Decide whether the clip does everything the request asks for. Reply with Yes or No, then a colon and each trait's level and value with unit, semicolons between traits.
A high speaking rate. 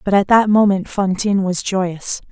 No: average, 180 wpm